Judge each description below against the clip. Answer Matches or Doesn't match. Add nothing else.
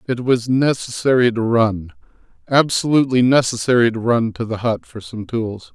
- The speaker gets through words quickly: Doesn't match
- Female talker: Doesn't match